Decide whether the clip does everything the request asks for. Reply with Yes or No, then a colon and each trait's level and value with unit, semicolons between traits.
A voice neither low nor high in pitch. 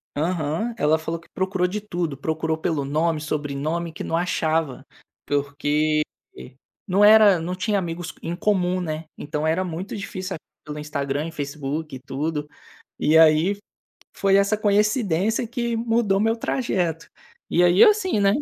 Yes: medium, 170 Hz